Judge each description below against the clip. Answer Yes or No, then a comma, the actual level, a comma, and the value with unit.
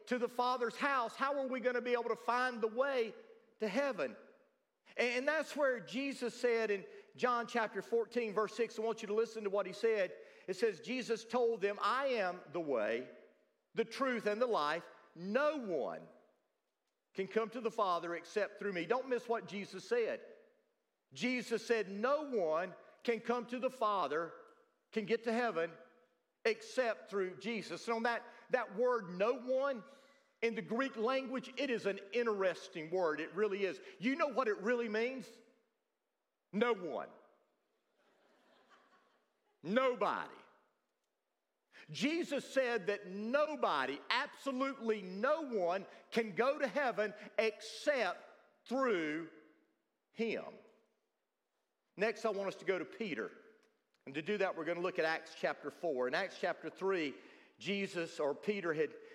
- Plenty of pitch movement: No, average, 4.6 semitones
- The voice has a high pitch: Yes, high, 230 Hz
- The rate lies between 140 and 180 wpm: Yes, average, 155 wpm